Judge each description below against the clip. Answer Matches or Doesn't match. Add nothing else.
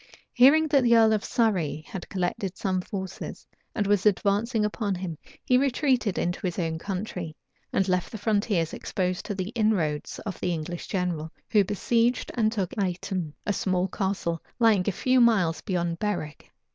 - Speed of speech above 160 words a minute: Matches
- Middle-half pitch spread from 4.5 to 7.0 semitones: Doesn't match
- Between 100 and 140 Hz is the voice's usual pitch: Doesn't match